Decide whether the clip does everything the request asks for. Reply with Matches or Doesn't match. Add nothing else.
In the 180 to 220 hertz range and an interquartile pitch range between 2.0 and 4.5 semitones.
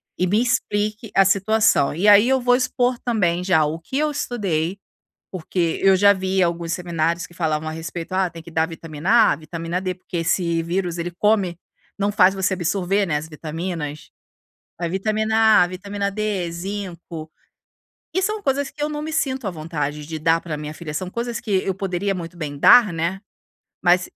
Matches